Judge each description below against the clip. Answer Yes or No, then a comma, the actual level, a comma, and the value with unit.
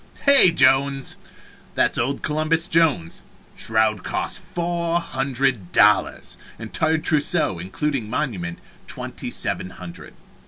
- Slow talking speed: Yes, slow, 110 wpm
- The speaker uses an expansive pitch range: Yes, wide, 6.9 semitones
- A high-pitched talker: No, low, 135 Hz